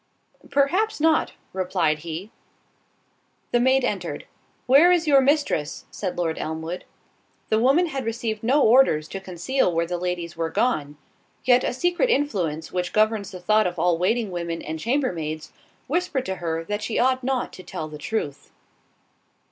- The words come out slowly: No, average, 165 wpm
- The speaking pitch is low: No, high, 210 Hz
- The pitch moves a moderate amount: No, wide, 7.7 semitones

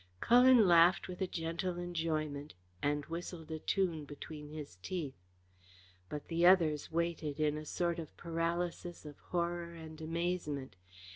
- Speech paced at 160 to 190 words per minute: No, average, 140 wpm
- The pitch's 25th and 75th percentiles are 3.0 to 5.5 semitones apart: No, narrow, 2.4 semitones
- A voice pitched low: No, medium, 165 Hz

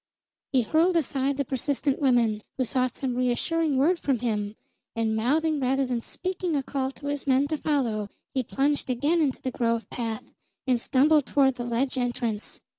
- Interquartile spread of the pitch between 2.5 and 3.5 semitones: Yes, average, 3.1 semitones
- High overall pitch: Yes, very high, 265 Hz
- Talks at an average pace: Yes, average, 180 wpm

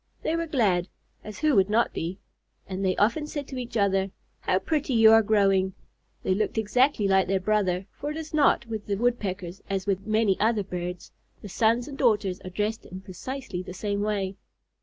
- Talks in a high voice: Yes, high, 205 Hz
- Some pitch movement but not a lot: Yes, average, 3.7 semitones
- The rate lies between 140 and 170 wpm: No, average, 200 wpm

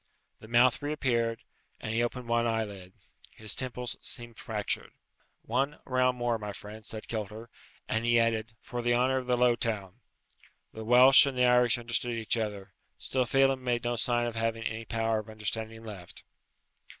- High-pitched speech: No, low, 115 Hz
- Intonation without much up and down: Yes, narrow, 1.9 semitones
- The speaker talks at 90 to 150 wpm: No, average, 175 wpm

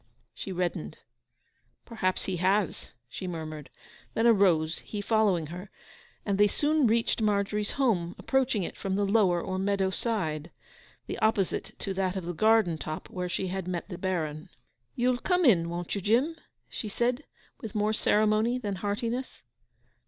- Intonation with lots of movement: No, average, 3.8 semitones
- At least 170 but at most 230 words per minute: No, average, 155 wpm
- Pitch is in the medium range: No, high, 200 Hz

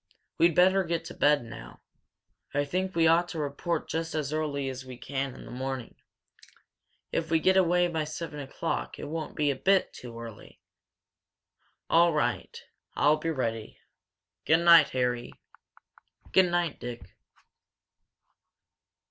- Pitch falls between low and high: Yes, medium, 150 Hz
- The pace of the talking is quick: No, average, 145 wpm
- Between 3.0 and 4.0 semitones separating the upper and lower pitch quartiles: No, average, 4.5 semitones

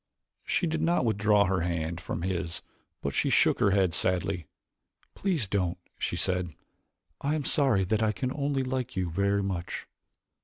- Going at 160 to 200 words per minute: Yes, average, 165 wpm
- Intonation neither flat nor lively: No, wide, 6.4 semitones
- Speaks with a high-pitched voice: No, low, 100 Hz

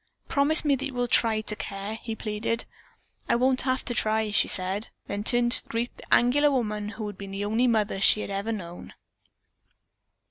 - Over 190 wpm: Yes, average, 200 wpm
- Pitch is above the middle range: Yes, high, 220 Hz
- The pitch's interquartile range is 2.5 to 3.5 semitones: Yes, average, 2.9 semitones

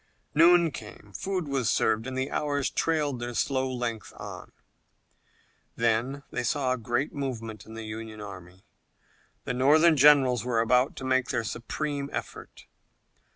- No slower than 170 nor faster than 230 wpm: No, average, 150 wpm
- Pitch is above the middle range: No, low, 130 Hz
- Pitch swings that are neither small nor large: Yes, average, 4.0 semitones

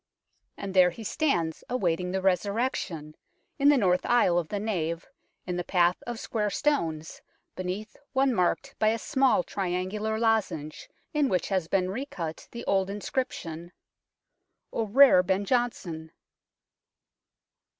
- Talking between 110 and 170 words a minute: Yes, average, 140 wpm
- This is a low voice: No, high, 195 Hz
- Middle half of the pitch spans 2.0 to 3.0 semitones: No, average, 4.8 semitones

